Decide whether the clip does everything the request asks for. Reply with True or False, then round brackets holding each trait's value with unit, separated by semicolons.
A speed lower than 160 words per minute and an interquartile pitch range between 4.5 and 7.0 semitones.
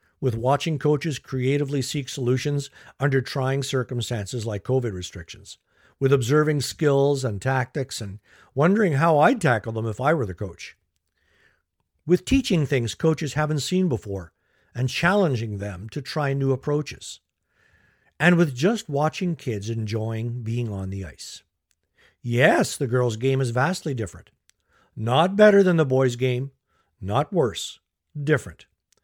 True (140 wpm; 5.0 semitones)